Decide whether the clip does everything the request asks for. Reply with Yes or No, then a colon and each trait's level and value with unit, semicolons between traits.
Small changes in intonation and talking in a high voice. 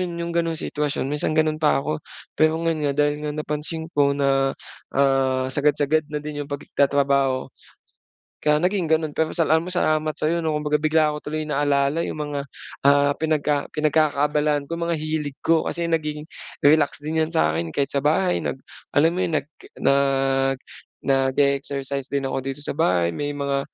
No: narrow, 2.0 semitones; medium, 150 Hz